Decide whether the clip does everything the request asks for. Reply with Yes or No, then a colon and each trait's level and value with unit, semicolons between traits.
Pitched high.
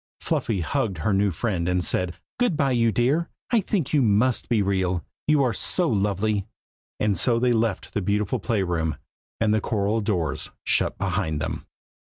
No: low, 105 Hz